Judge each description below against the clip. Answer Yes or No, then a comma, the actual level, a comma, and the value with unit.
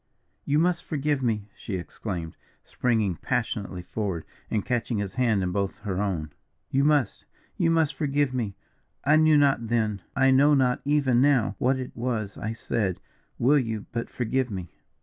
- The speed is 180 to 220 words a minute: No, average, 170 wpm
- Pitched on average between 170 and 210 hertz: No, low, 120 Hz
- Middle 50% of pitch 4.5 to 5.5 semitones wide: Yes, average, 5.2 semitones